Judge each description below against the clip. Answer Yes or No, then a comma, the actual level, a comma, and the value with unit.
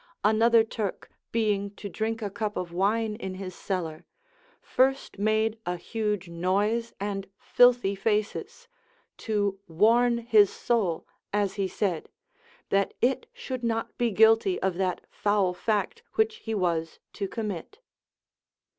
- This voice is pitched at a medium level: No, high, 210 Hz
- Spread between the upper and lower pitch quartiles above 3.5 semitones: No, average, 2.8 semitones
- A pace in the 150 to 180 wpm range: No, slow, 135 wpm